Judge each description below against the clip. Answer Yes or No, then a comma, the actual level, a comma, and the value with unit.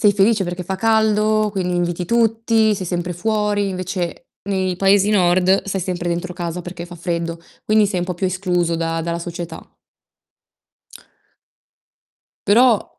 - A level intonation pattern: No, average, 3.0 semitones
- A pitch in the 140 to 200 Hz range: Yes, medium, 185 Hz